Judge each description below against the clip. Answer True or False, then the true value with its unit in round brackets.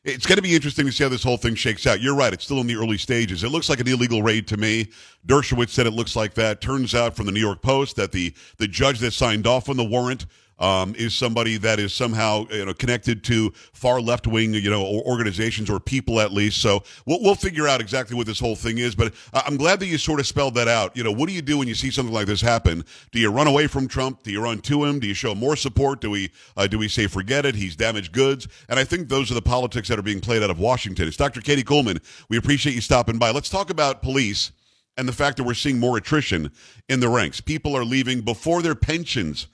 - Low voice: True (120 Hz)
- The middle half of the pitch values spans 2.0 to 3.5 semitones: False (3.9 semitones)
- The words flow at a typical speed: False (280 wpm)